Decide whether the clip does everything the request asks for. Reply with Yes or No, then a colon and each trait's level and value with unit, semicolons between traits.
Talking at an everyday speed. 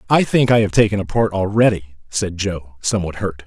No: fast, 210 wpm